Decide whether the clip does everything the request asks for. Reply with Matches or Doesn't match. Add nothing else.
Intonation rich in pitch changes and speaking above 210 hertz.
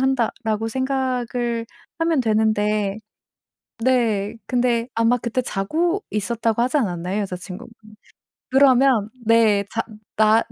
Doesn't match